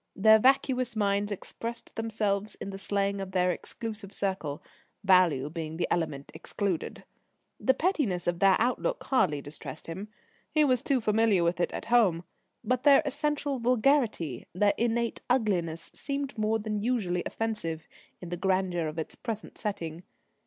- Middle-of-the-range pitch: No, high, 205 Hz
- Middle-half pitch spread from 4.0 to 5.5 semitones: Yes, average, 5.2 semitones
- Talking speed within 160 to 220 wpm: No, average, 150 wpm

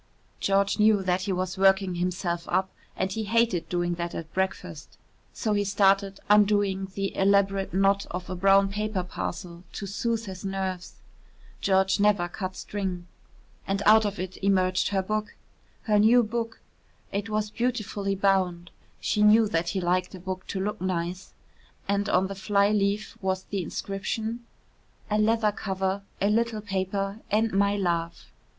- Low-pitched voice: No, high, 195 Hz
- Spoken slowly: No, average, 160 wpm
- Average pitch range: No, narrow, 2.0 semitones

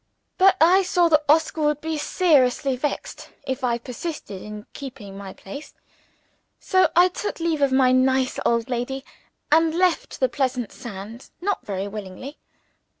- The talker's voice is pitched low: No, very high, 270 Hz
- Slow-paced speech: No, average, 150 wpm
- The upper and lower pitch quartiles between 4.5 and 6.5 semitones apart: Yes, average, 5.3 semitones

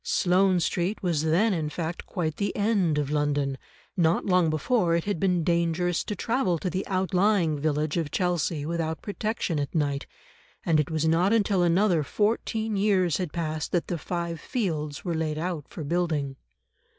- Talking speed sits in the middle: Yes, average, 175 wpm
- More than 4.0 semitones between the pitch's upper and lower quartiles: No, average, 3.3 semitones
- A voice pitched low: No, medium, 170 Hz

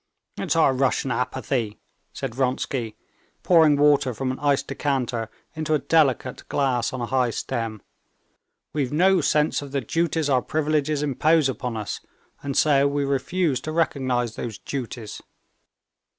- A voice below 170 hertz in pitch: Yes, low, 135 Hz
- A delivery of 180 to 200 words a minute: No, average, 145 wpm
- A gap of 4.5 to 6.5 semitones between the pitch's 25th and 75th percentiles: No, average, 3.1 semitones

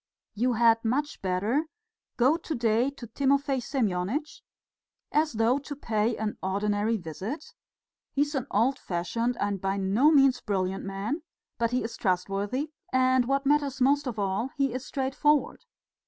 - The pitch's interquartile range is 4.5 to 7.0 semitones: Yes, average, 5.2 semitones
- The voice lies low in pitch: No, high, 240 Hz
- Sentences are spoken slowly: No, average, 155 wpm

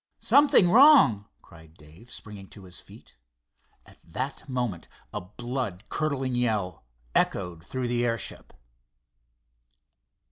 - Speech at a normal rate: No, slow, 110 wpm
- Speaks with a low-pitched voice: Yes, low, 115 Hz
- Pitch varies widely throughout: Yes, wide, 6.1 semitones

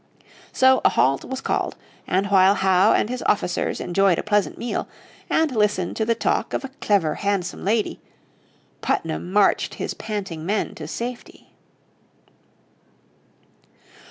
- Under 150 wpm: Yes, slow, 135 wpm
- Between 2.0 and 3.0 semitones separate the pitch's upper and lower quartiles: No, average, 3.5 semitones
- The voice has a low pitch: No, high, 200 Hz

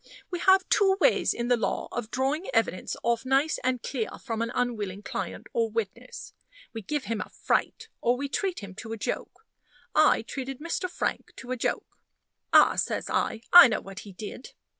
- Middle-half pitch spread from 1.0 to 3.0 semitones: No, average, 3.9 semitones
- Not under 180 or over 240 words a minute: Yes, average, 190 wpm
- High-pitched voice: Yes, high, 245 Hz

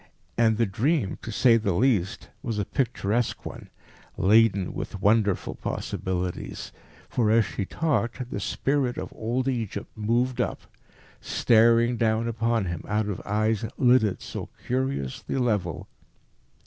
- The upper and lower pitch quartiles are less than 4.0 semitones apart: Yes, average, 3.0 semitones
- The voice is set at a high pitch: No, low, 115 Hz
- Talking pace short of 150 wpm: Yes, slow, 135 wpm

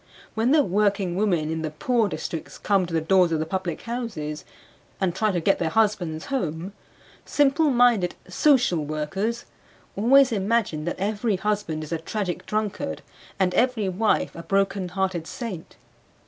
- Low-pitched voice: No, high, 195 Hz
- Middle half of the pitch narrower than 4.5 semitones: No, average, 5.0 semitones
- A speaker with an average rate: Yes, average, 160 wpm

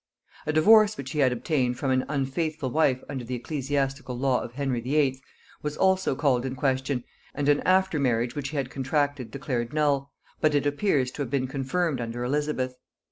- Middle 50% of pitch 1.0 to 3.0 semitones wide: Yes, narrow, 2.5 semitones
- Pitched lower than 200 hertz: Yes, low, 135 Hz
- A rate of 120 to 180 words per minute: No, average, 190 wpm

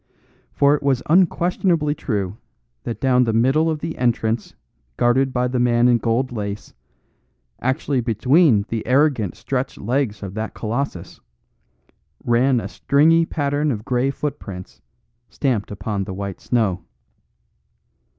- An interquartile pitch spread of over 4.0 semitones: Yes, average, 4.4 semitones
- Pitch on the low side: Yes, low, 125 Hz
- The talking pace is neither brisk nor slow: No, slow, 130 wpm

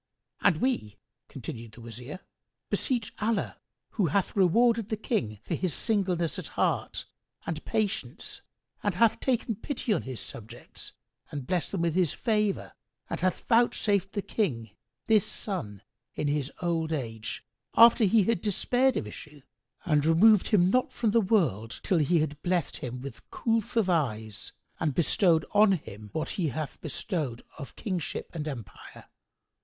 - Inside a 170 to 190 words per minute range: No, average, 155 wpm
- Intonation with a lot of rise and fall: Yes, wide, 7.4 semitones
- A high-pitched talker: No, medium, 175 Hz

